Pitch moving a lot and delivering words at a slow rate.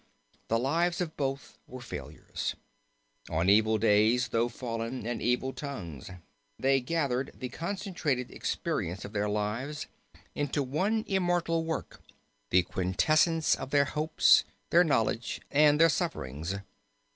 Yes: wide, 6.3 semitones; slow, 125 wpm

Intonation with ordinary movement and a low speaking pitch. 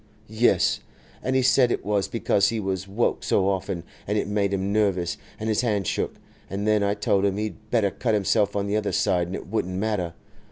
No: narrow, 1.9 semitones; low, 100 Hz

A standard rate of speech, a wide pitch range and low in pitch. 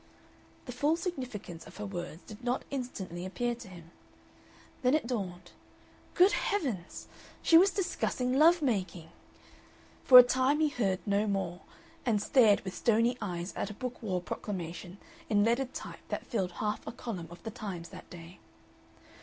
No: average, 160 wpm; wide, 5.7 semitones; high, 215 Hz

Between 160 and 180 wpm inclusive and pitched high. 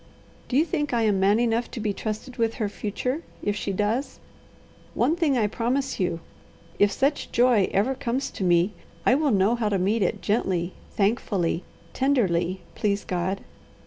Yes: average, 175 wpm; high, 215 Hz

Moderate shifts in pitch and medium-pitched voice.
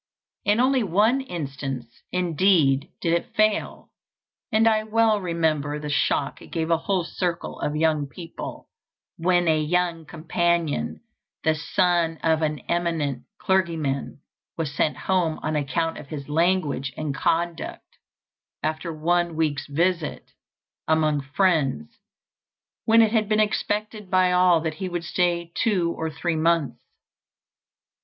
Yes: average, 3.2 semitones; medium, 165 Hz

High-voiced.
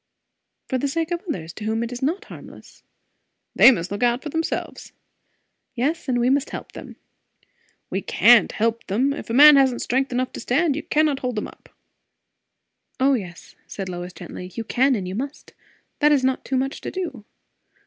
Yes: very high, 255 Hz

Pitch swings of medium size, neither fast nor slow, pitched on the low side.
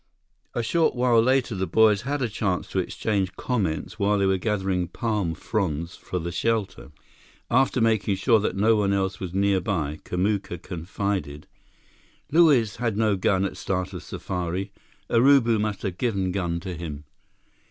Yes: average, 3.7 semitones; average, 160 wpm; low, 100 Hz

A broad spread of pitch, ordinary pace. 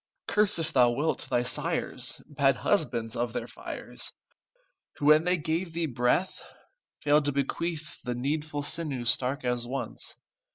No: average, 4.4 semitones; average, 150 wpm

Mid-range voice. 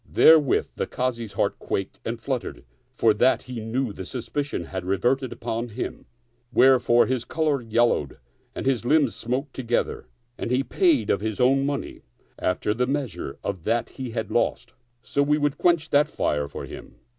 No: low, 125 Hz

